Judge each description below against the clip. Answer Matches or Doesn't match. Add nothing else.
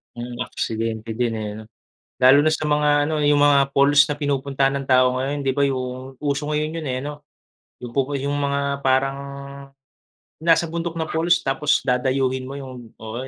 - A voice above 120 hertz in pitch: Matches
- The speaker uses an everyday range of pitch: Doesn't match